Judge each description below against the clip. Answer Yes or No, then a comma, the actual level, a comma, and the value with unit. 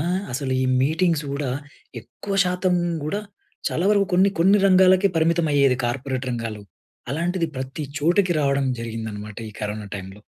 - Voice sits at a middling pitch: Yes, medium, 150 Hz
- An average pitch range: No, wide, 6.8 semitones